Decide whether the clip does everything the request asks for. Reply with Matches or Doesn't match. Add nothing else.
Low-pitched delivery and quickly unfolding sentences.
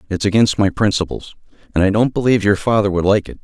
Matches